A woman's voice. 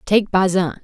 Yes: female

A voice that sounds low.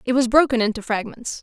No: high, 240 Hz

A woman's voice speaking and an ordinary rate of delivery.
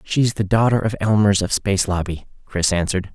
No: male; average, 190 wpm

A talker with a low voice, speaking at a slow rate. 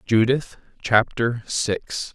Yes: low, 115 Hz; slow, 85 wpm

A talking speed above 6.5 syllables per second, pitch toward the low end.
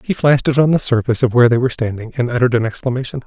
Yes: 8.3 syllables/s; low, 125 Hz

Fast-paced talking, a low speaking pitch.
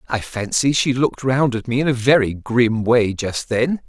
Yes: fast, 215 wpm; low, 125 Hz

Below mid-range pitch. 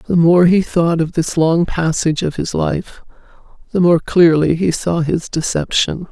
No: medium, 170 Hz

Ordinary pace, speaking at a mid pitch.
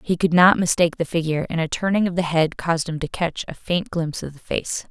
No: fast, 270 wpm; medium, 170 Hz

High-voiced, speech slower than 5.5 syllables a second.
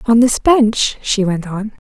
Yes: high, 220 Hz; 3.8 syllables/s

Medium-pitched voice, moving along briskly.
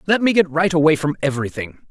Yes: medium, 160 Hz; fast, 220 wpm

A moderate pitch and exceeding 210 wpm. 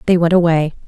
No: medium, 170 Hz; fast, 205 wpm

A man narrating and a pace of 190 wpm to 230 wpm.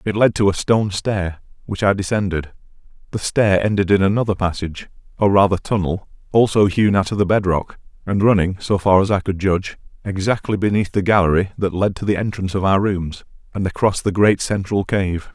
Yes: male; average, 200 wpm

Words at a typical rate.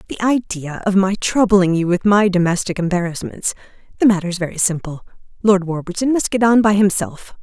Yes: average, 170 wpm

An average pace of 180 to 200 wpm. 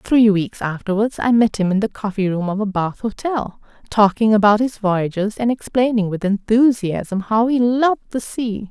Yes: average, 185 wpm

